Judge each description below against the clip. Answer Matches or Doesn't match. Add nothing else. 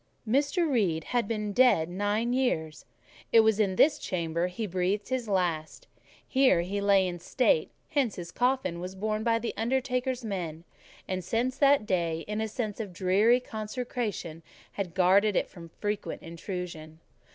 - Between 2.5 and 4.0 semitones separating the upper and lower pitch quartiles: Doesn't match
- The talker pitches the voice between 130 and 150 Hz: Doesn't match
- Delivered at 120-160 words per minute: Matches